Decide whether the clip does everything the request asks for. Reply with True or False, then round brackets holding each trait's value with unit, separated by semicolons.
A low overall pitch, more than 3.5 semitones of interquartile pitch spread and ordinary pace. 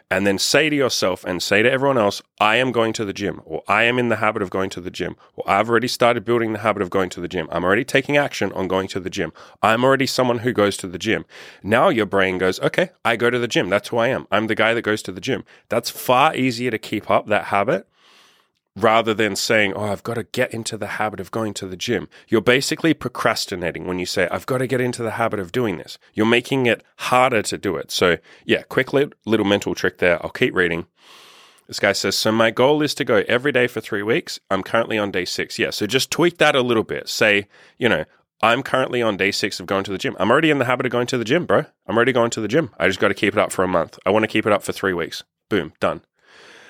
False (110 Hz; 4.0 semitones; 275 wpm)